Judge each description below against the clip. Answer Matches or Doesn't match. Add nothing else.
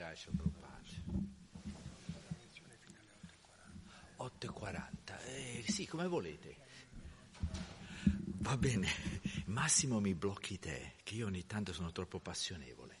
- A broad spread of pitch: Matches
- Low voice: Matches